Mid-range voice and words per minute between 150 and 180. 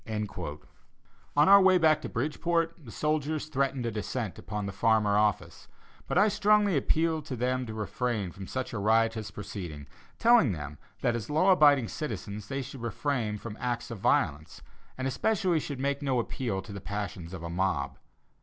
No: low, 120 Hz; average, 175 wpm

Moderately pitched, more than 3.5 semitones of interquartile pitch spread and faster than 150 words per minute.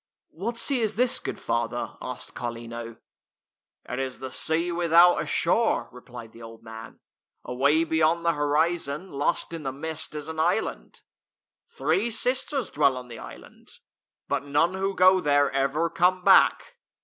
Yes: medium, 160 Hz; average, 5.2 semitones; average, 160 wpm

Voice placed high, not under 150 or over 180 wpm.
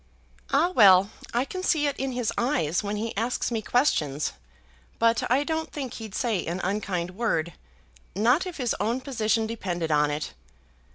Yes: high, 225 Hz; average, 170 wpm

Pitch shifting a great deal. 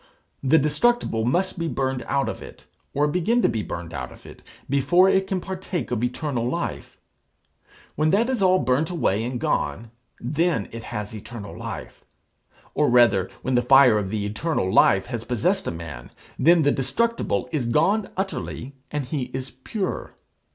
Yes: wide, 7.2 semitones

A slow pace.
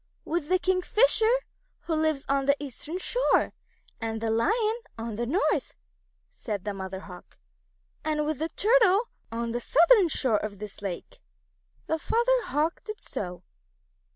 No: average, 160 wpm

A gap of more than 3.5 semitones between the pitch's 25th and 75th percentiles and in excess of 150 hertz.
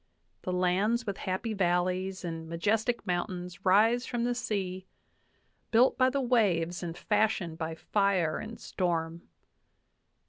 Yes: average, 3.9 semitones; medium, 185 Hz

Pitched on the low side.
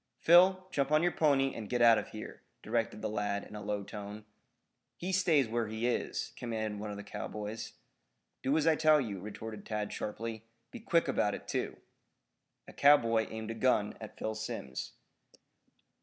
Yes: low, 115 Hz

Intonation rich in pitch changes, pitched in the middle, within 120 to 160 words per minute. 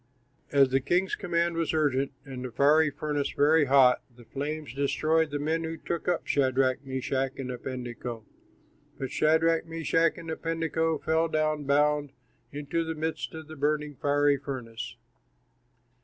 No: average, 3.1 semitones; medium, 145 Hz; average, 145 wpm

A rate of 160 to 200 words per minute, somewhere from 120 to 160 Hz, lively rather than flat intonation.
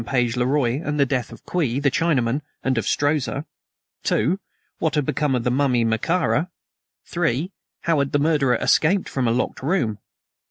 No: average, 185 wpm; medium, 140 Hz; average, 3.7 semitones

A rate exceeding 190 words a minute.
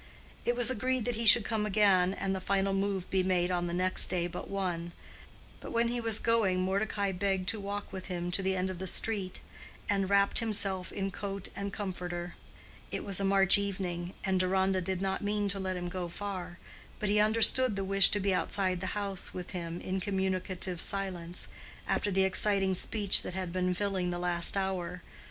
Yes: average, 200 wpm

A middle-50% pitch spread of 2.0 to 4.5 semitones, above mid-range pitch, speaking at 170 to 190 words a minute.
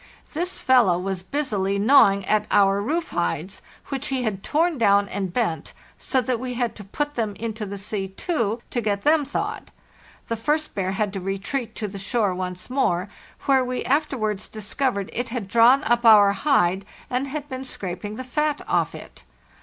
No: average, 5.0 semitones; high, 220 Hz; average, 185 wpm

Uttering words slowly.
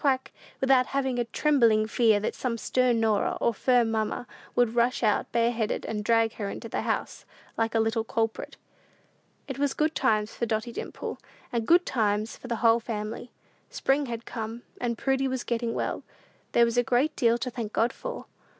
No: average, 190 wpm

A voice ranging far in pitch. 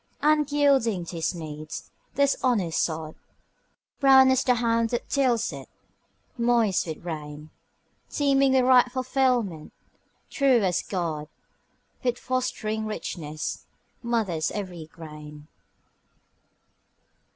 Yes: wide, 8.0 semitones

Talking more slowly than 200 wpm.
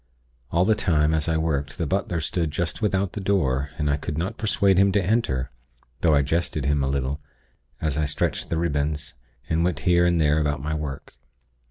No: fast, 205 wpm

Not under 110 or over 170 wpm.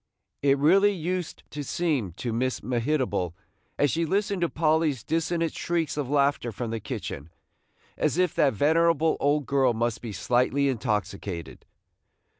Yes: average, 145 wpm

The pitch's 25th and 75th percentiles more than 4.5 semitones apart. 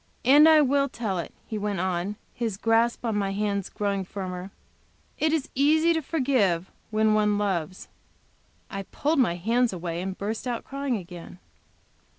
Yes: average, 5.2 semitones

